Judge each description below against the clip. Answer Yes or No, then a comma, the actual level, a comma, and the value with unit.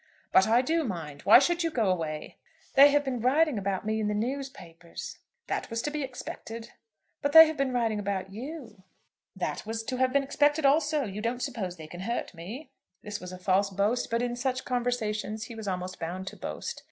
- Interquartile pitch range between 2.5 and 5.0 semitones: No, wide, 5.6 semitones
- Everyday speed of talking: No, fast, 210 wpm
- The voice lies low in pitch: No, high, 230 Hz